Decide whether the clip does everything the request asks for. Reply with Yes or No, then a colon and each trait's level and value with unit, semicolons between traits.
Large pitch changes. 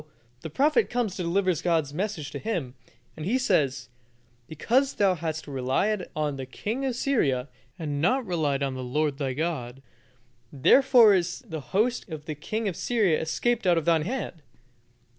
Yes: wide, 6.9 semitones